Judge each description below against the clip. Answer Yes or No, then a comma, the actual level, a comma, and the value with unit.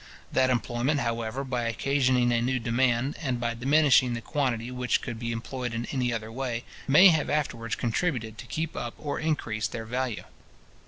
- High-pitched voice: No, low, 125 Hz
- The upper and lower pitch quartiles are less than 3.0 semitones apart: Yes, narrow, 2.5 semitones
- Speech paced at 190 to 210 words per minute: No, average, 175 wpm